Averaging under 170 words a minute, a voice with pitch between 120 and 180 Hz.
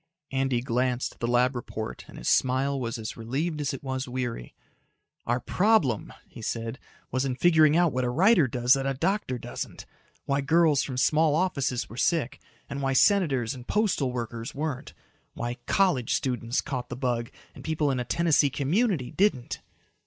No: average, 175 wpm; low, 135 Hz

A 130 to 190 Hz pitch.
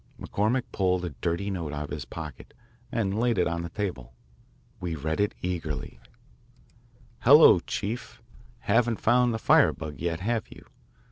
No: very low, 90 Hz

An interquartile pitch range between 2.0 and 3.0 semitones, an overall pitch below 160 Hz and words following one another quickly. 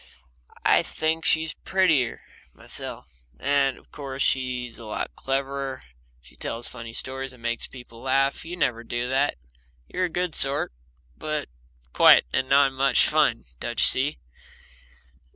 No: narrow, 2.6 semitones; low, 135 Hz; average, 145 wpm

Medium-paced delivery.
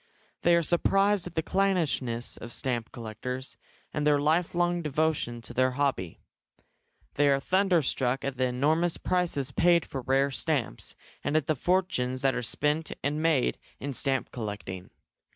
Yes: average, 150 wpm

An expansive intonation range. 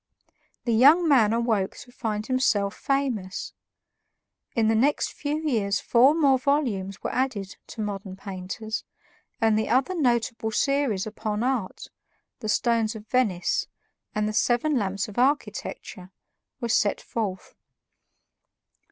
No: average, 3.9 semitones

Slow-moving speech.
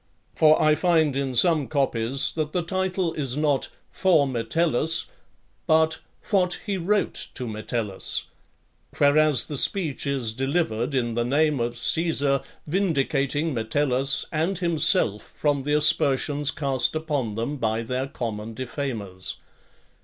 Yes: slow, 130 wpm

